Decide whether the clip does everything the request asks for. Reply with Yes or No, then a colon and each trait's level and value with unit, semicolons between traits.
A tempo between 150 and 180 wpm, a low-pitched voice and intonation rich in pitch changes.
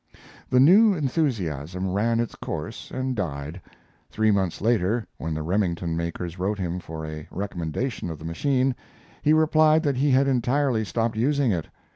Yes: average, 165 wpm; low, 110 Hz; wide, 7.7 semitones